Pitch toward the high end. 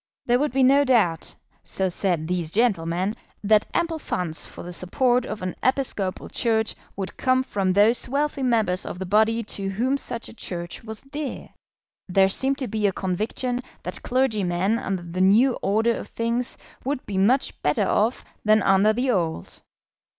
Yes: high, 215 Hz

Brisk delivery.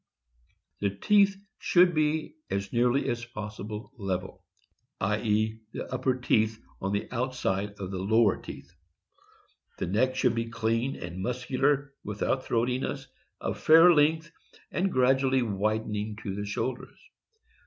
No: slow, 135 wpm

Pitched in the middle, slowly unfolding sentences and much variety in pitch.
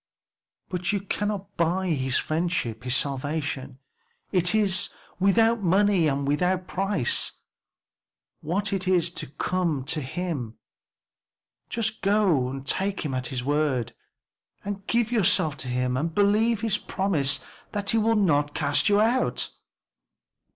Yes: medium, 180 Hz; slow, 130 wpm; wide, 6.2 semitones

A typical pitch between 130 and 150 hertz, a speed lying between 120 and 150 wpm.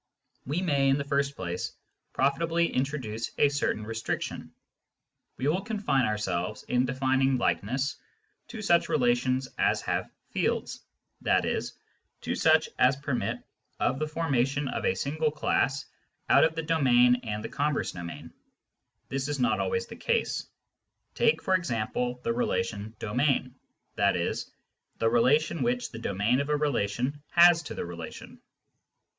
Yes: low, 135 Hz; average, 145 wpm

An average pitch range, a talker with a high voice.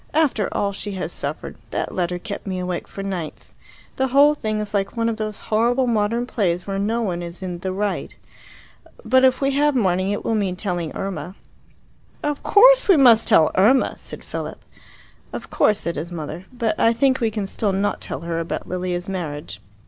Yes: average, 4.5 semitones; high, 205 Hz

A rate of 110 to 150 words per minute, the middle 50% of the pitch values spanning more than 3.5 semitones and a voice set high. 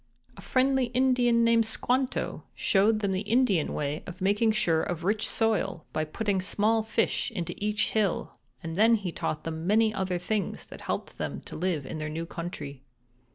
No: average, 175 wpm; average, 5.1 semitones; high, 200 Hz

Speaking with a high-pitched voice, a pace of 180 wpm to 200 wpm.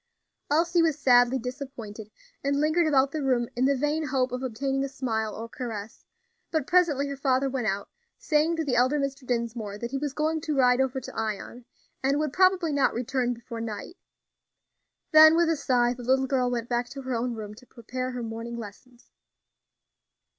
Yes: very high, 260 Hz; average, 190 wpm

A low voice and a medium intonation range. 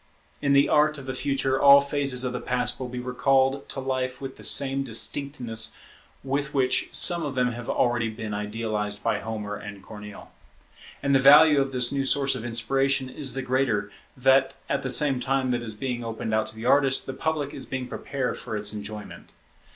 Yes: low, 130 Hz; average, 3.1 semitones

